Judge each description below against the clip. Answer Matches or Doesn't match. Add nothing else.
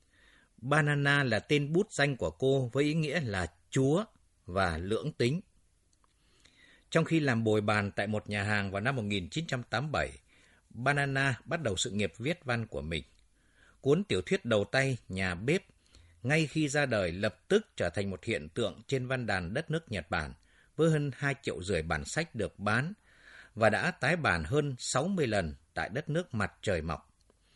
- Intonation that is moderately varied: Doesn't match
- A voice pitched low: Matches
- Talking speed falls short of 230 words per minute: Matches